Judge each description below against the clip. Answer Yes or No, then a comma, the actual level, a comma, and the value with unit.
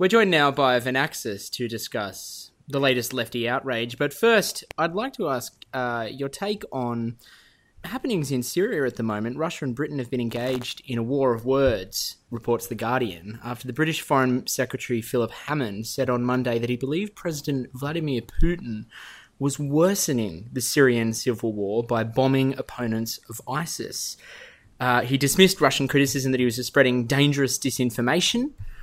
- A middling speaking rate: Yes, average, 165 wpm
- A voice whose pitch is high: No, low, 130 Hz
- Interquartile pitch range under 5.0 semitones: Yes, average, 3.1 semitones